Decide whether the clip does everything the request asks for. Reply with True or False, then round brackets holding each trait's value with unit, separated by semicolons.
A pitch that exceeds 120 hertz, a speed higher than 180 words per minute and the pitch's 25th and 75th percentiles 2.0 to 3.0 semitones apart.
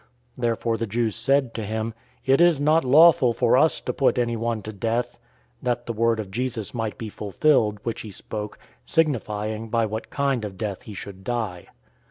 False (115 Hz; 190 wpm; 2.7 semitones)